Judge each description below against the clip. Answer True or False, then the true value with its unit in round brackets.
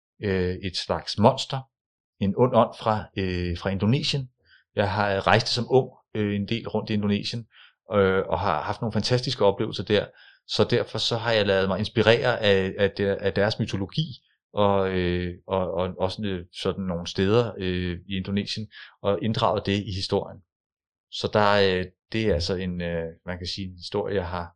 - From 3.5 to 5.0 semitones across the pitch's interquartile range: False (2.7 semitones)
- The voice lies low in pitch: True (100 Hz)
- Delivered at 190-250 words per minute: False (180 wpm)